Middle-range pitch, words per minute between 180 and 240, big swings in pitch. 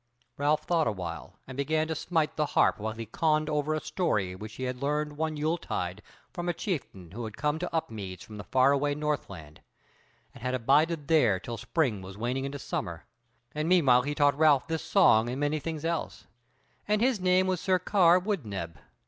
Yes: medium, 145 Hz; average, 200 wpm; wide, 6.4 semitones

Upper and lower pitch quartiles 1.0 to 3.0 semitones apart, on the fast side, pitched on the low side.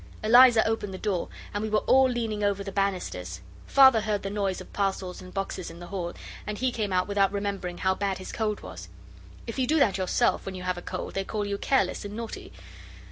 No: narrow, 2.5 semitones; fast, 230 wpm; high, 200 Hz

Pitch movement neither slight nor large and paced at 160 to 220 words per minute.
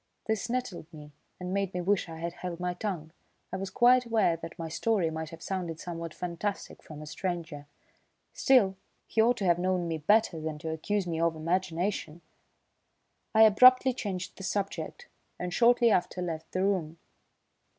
Yes: average, 3.8 semitones; average, 175 wpm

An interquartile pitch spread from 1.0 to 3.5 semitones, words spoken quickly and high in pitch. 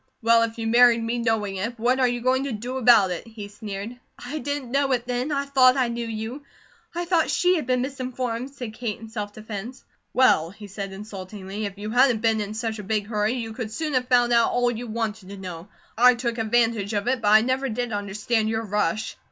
Yes: average, 2.9 semitones; fast, 230 wpm; high, 230 Hz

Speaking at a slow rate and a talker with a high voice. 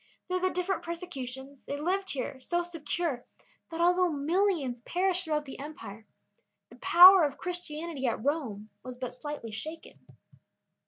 No: average, 145 wpm; very high, 310 Hz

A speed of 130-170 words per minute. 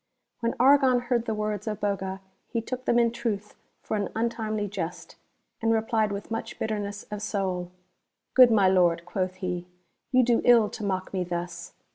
No: average, 190 wpm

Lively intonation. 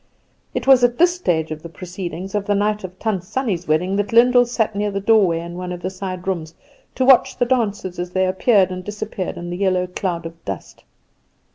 No: average, 3.4 semitones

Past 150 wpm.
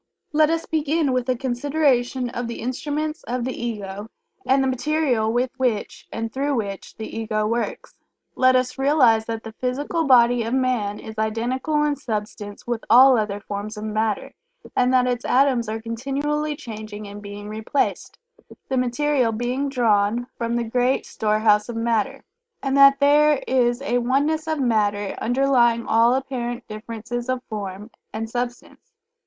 Yes: average, 160 wpm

